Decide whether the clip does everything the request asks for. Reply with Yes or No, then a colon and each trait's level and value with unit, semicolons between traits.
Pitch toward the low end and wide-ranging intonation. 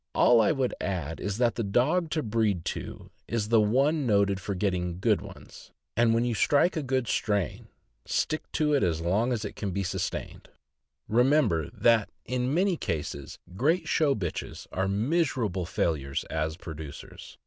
Yes: low, 110 Hz; wide, 6.3 semitones